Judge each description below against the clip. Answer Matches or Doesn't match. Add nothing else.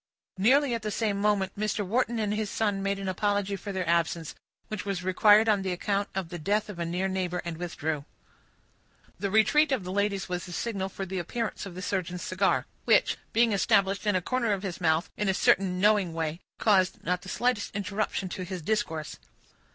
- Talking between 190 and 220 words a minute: Matches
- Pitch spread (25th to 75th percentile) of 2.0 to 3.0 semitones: Matches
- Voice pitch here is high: Matches